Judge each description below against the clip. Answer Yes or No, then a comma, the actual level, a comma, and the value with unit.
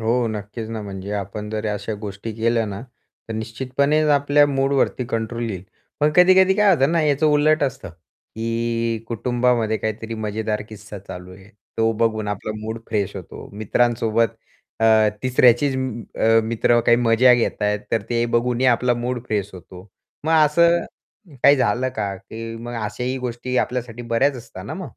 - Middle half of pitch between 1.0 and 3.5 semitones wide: Yes, average, 2.9 semitones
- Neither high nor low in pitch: No, low, 115 Hz